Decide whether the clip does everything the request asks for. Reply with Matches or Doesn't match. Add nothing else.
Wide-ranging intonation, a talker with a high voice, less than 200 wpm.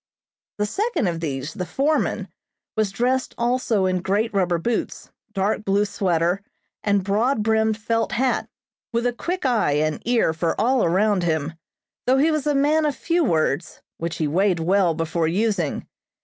Matches